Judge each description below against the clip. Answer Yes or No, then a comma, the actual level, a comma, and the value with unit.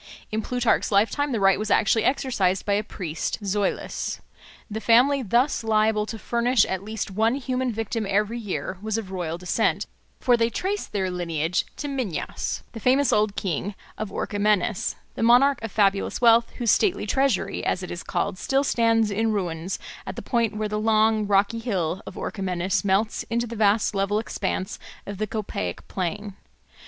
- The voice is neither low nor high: No, high, 215 Hz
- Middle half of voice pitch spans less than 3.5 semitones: Yes, average, 3.0 semitones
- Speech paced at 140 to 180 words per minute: Yes, average, 175 wpm